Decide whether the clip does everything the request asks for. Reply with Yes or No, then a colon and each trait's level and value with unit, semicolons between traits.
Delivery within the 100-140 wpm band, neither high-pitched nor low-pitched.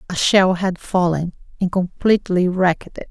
No: average, 155 wpm; medium, 180 Hz